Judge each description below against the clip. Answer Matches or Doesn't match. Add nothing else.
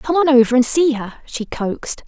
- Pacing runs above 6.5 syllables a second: Doesn't match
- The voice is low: Doesn't match